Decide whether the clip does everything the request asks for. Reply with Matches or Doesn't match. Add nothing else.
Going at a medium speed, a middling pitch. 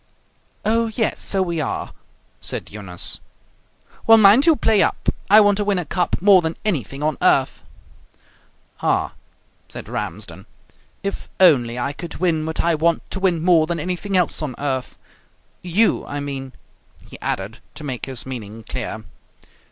Matches